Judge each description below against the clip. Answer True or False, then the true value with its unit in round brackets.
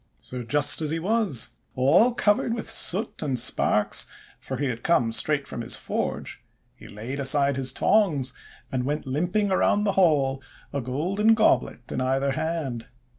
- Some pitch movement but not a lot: False (6.4 semitones)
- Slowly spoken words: False (165 wpm)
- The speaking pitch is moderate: True (145 Hz)